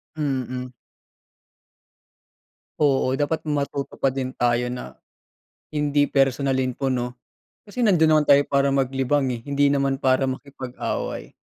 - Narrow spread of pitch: Yes, narrow, 1.8 semitones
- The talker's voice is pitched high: No, low, 135 Hz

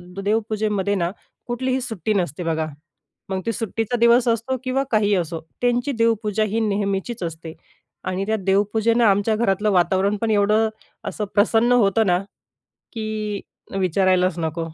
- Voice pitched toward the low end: No, high, 210 Hz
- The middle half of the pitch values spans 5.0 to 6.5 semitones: No, average, 3.2 semitones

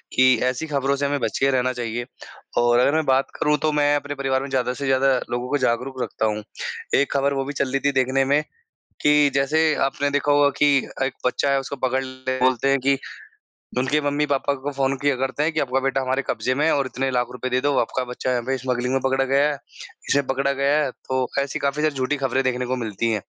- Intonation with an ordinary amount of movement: No, narrow, 1.7 semitones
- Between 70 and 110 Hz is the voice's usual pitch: No, low, 135 Hz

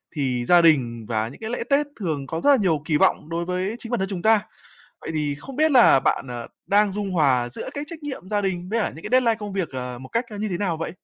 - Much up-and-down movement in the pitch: Yes, wide, 7.5 semitones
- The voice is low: No, medium, 180 Hz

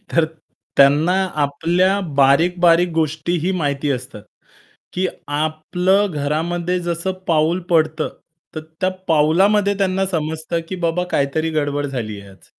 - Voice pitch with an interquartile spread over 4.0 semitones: No, average, 3.5 semitones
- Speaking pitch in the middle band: Yes, medium, 160 Hz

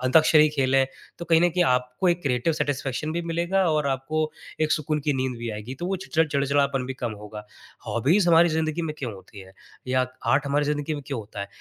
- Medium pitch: Yes, medium, 145 Hz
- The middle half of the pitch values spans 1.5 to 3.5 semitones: No, average, 3.9 semitones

